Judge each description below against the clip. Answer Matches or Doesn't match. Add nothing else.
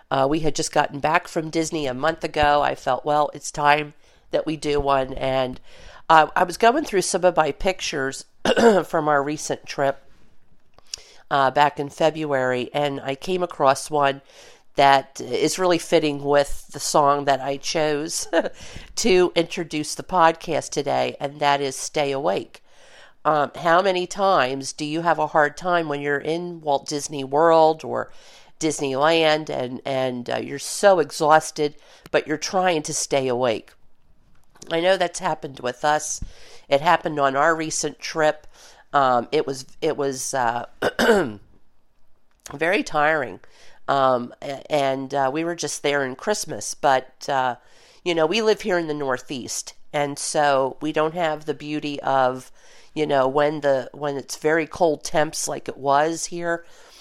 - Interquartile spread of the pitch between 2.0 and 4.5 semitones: Matches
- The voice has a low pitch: Doesn't match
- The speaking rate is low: Doesn't match